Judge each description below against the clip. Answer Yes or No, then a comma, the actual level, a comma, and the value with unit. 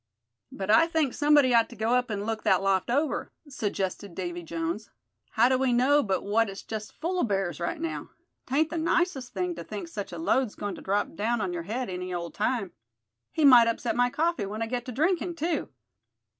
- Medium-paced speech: No, fast, 215 wpm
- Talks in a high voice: Yes, high, 225 Hz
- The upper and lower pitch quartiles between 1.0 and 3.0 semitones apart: No, wide, 5.6 semitones